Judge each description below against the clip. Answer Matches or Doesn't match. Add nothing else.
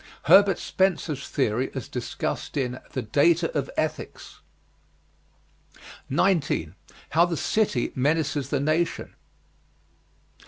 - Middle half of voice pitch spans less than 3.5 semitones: Doesn't match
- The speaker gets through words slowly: Matches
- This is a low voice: Doesn't match